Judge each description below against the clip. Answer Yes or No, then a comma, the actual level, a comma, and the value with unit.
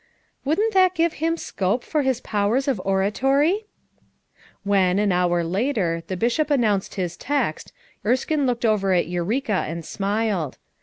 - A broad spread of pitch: Yes, wide, 6.7 semitones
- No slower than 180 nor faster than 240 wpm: No, average, 145 wpm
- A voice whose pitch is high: Yes, high, 215 Hz